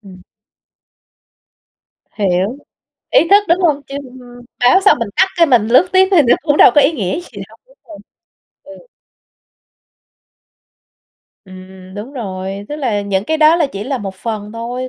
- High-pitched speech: Yes, high, 245 Hz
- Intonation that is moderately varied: No, wide, 7.5 semitones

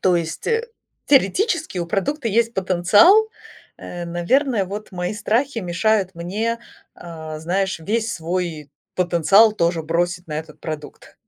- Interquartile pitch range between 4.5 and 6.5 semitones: Yes, average, 4.9 semitones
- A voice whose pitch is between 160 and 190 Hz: Yes, medium, 185 Hz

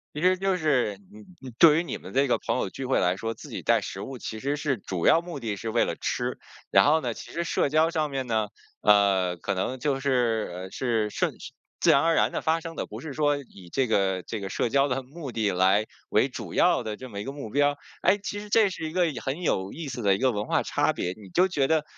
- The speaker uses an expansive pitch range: Yes, wide, 6.7 semitones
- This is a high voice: No, low, 130 Hz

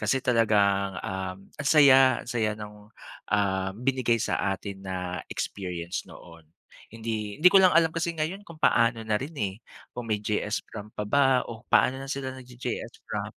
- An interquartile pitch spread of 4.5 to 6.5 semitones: Yes, average, 4.8 semitones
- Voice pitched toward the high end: No, low, 110 Hz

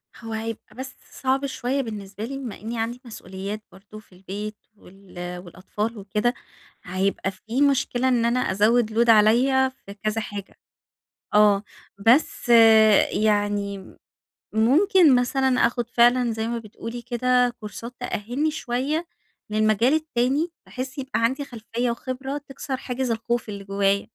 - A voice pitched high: Yes, high, 235 Hz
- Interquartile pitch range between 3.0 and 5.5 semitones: Yes, average, 3.7 semitones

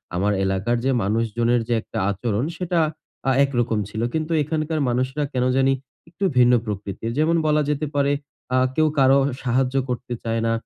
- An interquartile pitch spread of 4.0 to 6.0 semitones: Yes, average, 4.4 semitones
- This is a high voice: No, low, 125 Hz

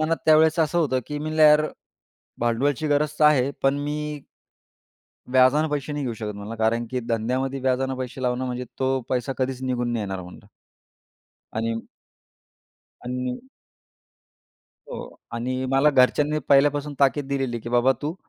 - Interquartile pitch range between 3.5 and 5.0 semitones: No, average, 3.1 semitones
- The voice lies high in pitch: No, low, 130 Hz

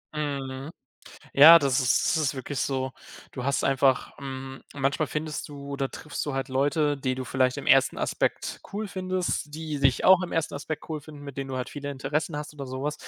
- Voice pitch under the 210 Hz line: Yes, medium, 140 Hz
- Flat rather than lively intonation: Yes, narrow, 2.2 semitones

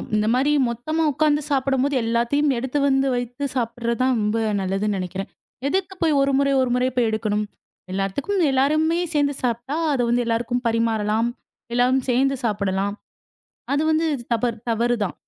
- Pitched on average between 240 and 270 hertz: Yes, high, 245 Hz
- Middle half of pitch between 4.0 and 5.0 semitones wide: No, average, 3.6 semitones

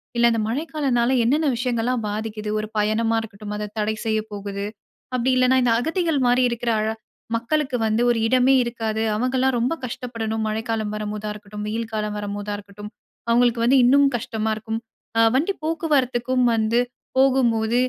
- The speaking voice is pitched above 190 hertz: Yes, high, 230 Hz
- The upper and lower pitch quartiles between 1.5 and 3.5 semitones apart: Yes, average, 2.8 semitones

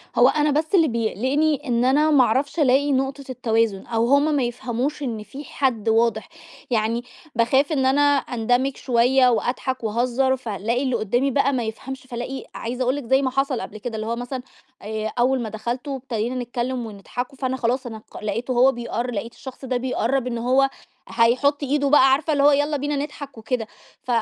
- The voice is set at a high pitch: Yes, very high, 255 Hz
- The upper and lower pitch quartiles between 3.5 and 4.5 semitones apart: No, average, 2.8 semitones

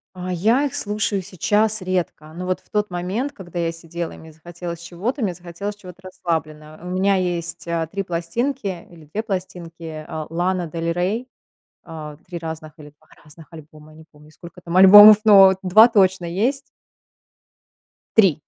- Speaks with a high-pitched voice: No, medium, 175 Hz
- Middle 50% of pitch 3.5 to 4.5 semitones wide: No, average, 3.1 semitones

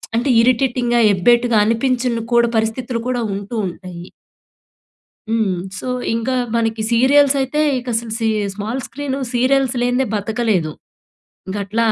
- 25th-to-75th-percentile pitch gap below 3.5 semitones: Yes, narrow, 2.4 semitones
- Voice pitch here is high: Yes, high, 235 Hz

